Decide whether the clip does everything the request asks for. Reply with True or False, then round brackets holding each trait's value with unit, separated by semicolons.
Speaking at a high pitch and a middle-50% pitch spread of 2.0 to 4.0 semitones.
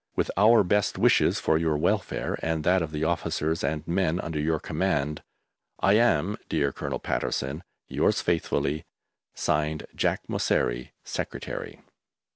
False (80 Hz; 3.2 semitones)